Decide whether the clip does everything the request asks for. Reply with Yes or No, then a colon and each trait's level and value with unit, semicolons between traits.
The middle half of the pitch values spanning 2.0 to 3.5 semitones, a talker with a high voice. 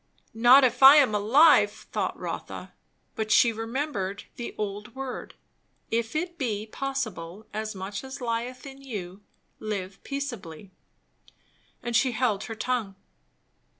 No: average, 4.3 semitones; high, 230 Hz